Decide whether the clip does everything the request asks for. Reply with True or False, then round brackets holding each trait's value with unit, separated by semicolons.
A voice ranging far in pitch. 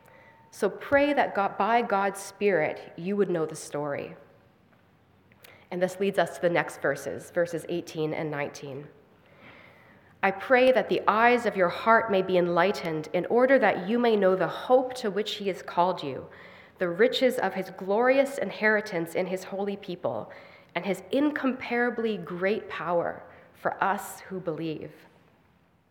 False (3.9 semitones)